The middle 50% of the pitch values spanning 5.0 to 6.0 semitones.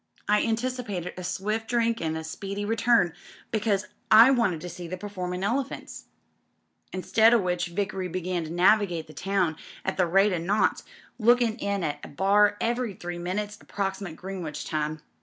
No: average, 3.5 semitones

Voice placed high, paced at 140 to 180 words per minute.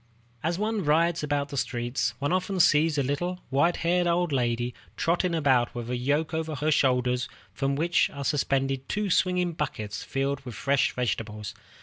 No: medium, 145 Hz; average, 175 wpm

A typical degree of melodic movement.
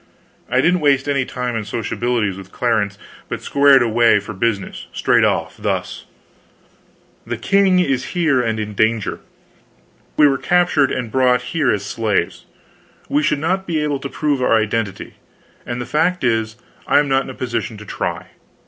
Yes: average, 4.6 semitones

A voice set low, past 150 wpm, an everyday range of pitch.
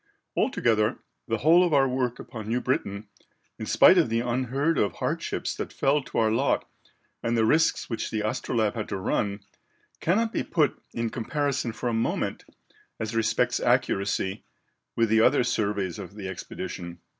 Yes: low, 115 Hz; average, 170 wpm; average, 3.5 semitones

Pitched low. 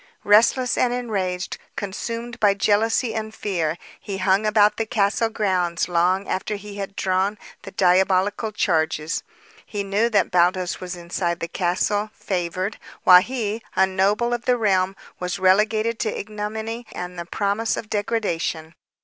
No: high, 200 Hz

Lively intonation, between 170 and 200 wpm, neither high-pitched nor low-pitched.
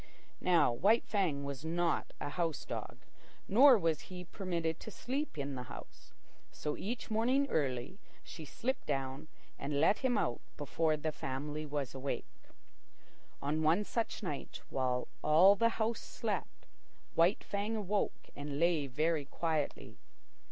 No: wide, 6.0 semitones; average, 145 wpm; medium, 160 Hz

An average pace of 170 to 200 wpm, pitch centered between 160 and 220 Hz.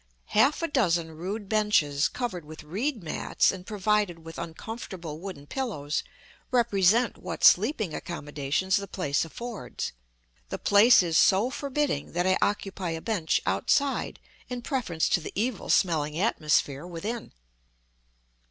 No: slow, 135 wpm; high, 190 Hz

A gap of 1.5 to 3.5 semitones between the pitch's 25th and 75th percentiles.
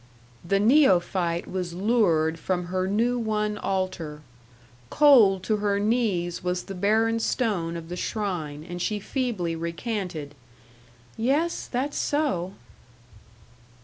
No: average, 4.5 semitones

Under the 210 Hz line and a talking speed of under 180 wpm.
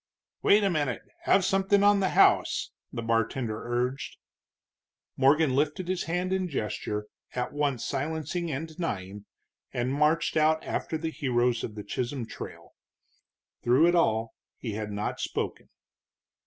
Yes: medium, 140 Hz; average, 140 wpm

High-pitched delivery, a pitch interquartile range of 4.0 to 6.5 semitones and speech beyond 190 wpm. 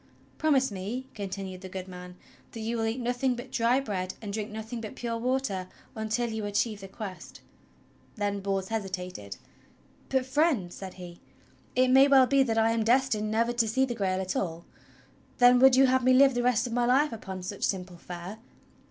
Yes: high, 225 Hz; average, 4.7 semitones; average, 200 wpm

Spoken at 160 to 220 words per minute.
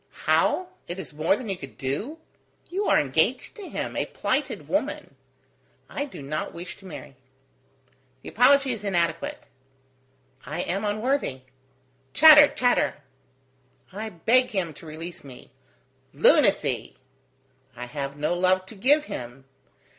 No: average, 140 wpm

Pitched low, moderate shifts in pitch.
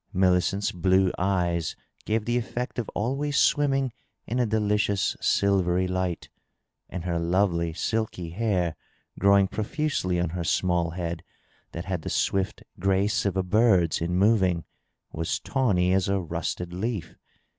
Yes: very low, 95 Hz; average, 3.4 semitones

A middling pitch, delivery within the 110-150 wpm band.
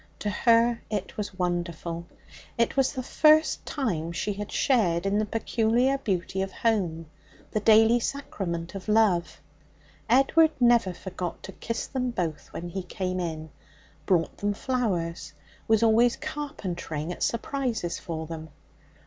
No: high, 205 Hz; average, 140 wpm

